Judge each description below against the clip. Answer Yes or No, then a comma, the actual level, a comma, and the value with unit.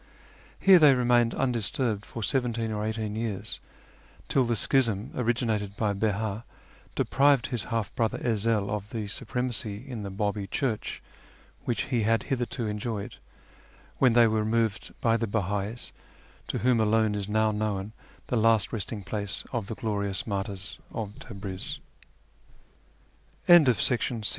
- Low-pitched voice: Yes, low, 110 Hz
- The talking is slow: Yes, slow, 130 wpm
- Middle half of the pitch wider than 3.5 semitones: No, narrow, 2.5 semitones